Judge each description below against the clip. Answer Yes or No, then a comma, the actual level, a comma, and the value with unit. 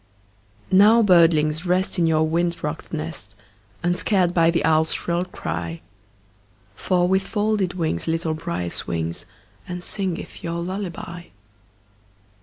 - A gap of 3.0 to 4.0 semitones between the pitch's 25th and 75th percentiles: No, narrow, 2.5 semitones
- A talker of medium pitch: Yes, medium, 170 Hz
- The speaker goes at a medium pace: No, slow, 120 wpm